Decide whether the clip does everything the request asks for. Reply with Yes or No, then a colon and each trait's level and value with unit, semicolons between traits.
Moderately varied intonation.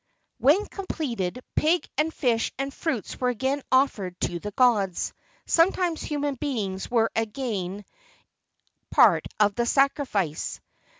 No: wide, 5.8 semitones